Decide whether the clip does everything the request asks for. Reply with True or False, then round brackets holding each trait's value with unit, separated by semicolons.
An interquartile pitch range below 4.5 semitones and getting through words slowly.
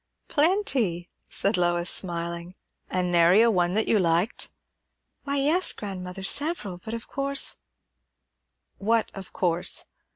False (4.9 semitones; 125 wpm)